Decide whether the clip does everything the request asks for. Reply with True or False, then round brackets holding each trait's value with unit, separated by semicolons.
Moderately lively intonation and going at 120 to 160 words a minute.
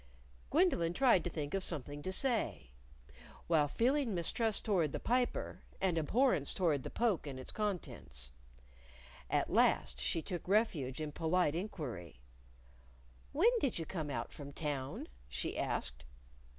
False (6.9 semitones; 140 wpm)